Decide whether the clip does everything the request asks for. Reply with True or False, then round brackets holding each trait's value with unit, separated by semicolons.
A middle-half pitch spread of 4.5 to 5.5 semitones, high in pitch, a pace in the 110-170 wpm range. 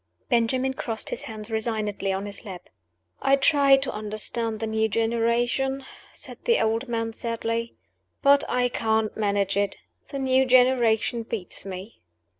False (3.0 semitones; 230 Hz; 145 wpm)